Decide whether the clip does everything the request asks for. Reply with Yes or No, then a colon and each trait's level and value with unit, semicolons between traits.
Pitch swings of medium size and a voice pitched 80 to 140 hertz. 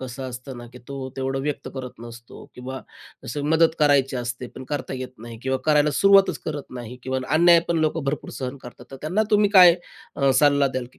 Yes: average, 3.1 semitones; low, 135 Hz